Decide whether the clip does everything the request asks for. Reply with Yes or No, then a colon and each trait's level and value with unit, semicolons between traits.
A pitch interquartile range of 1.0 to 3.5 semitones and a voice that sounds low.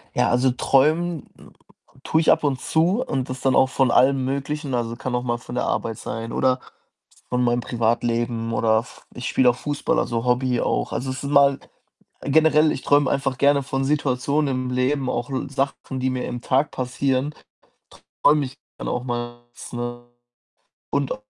Yes: narrow, 2.5 semitones; low, 130 Hz